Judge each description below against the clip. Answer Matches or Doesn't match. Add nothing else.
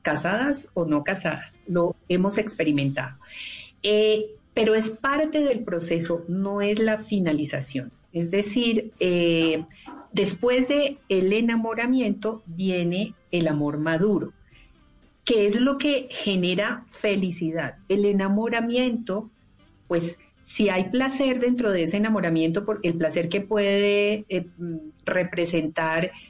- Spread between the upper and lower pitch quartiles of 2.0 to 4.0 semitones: Doesn't match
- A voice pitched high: Matches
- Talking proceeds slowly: Matches